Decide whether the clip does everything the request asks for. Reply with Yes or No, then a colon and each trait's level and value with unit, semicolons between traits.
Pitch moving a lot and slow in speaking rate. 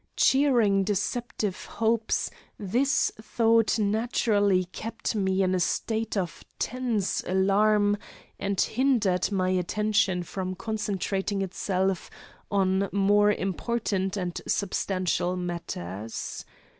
No: average, 2.8 semitones; slow, 95 wpm